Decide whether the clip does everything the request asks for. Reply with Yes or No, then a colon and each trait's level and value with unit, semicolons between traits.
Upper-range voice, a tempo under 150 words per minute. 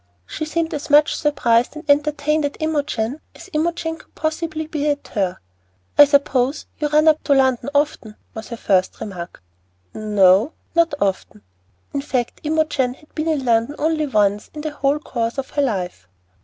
No: very high, 285 Hz; average, 175 wpm